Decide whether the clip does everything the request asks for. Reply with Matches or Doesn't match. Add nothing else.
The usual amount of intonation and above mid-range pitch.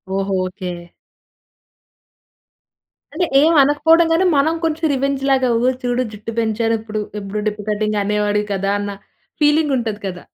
Doesn't match